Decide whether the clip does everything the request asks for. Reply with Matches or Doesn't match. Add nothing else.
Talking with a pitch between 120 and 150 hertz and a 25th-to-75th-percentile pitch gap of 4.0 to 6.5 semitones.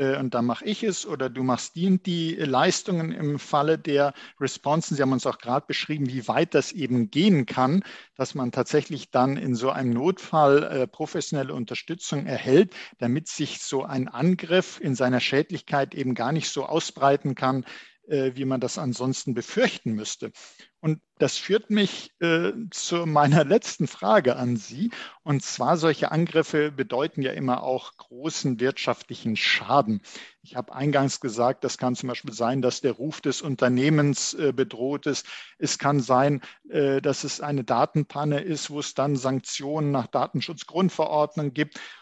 Doesn't match